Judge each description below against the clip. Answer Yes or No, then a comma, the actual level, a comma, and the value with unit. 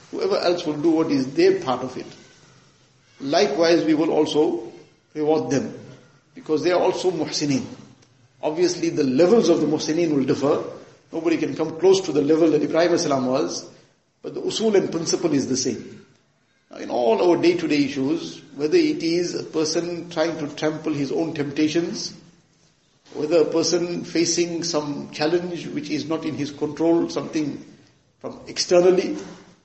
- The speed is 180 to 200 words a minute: No, average, 160 wpm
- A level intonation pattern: No, average, 3.0 semitones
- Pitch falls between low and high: Yes, medium, 165 Hz